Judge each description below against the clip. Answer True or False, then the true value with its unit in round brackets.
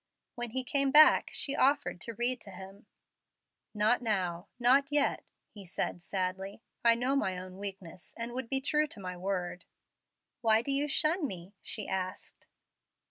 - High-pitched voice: True (225 Hz)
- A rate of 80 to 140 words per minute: False (165 wpm)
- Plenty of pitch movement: True (5.9 semitones)